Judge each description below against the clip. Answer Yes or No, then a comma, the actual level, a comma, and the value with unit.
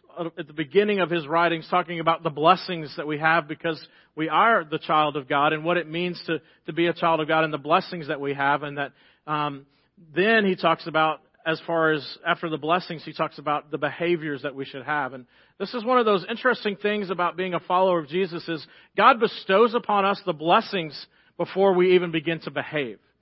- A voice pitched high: No, medium, 165 Hz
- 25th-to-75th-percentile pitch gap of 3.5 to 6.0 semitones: No, average, 2.9 semitones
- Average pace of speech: No, fast, 220 wpm